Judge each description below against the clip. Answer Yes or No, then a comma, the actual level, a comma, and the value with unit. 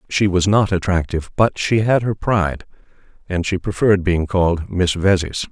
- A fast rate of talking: No, average, 175 wpm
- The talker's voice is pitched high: No, very low, 95 Hz